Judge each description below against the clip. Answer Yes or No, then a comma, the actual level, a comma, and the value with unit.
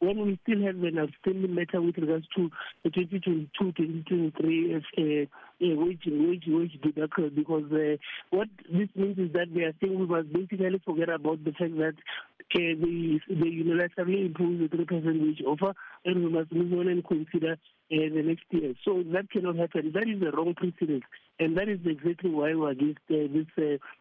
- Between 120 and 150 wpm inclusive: No, fast, 205 wpm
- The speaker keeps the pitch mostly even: Yes, narrow, 2.3 semitones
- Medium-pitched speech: Yes, medium, 170 Hz